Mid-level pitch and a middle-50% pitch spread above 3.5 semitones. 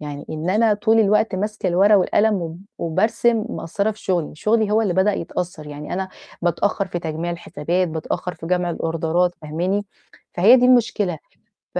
Yes: medium, 180 Hz; average, 4.2 semitones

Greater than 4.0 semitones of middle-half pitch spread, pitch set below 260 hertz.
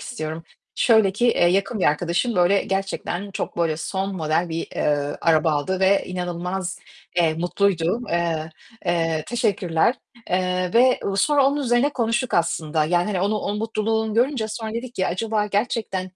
Yes: average, 4.5 semitones; high, 190 Hz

